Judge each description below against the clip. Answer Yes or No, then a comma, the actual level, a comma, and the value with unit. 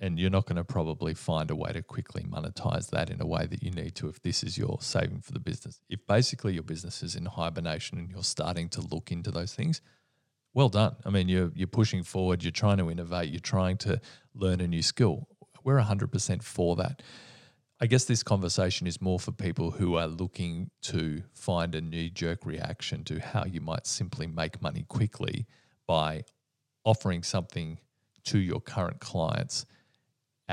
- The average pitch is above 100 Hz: No, very low, 95 Hz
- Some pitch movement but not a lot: No, wide, 6.3 semitones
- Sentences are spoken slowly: No, average, 195 wpm